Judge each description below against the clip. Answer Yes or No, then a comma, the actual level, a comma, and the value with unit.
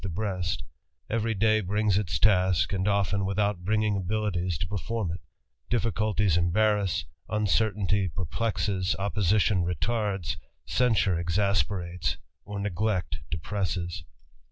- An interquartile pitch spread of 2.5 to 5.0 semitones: Yes, average, 2.9 semitones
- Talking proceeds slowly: Yes, slow, 105 wpm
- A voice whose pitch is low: Yes, low, 100 Hz